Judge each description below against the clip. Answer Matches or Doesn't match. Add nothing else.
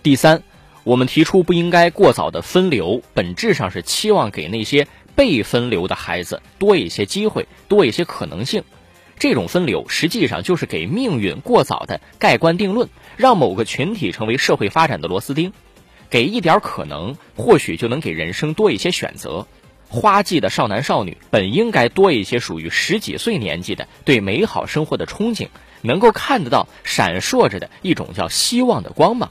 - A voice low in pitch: Doesn't match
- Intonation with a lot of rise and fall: Matches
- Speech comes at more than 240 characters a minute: Matches